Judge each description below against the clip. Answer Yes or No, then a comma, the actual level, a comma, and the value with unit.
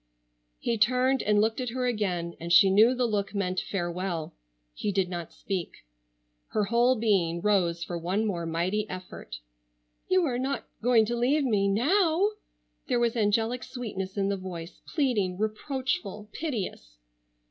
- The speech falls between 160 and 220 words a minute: No, average, 150 wpm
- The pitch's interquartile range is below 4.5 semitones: No, average, 4.9 semitones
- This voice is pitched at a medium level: No, high, 210 Hz